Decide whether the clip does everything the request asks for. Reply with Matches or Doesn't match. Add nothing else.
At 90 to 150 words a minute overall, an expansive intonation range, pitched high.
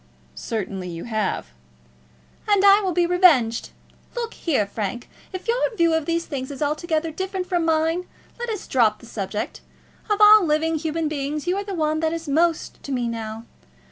Doesn't match